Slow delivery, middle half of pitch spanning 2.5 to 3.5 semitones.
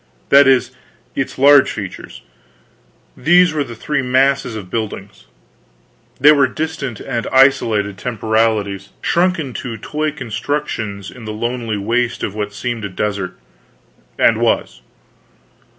No: slow, 125 wpm; average, 4.7 semitones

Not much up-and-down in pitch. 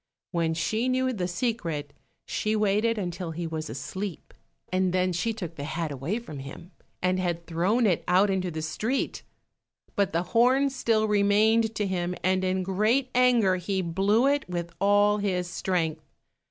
No: average, 4.0 semitones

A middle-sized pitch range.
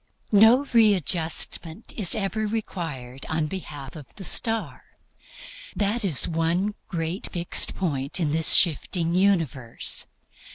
Yes: average, 4.4 semitones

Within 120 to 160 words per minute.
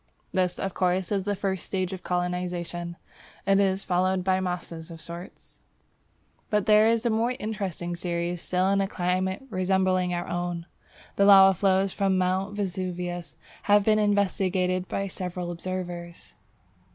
Yes: average, 150 wpm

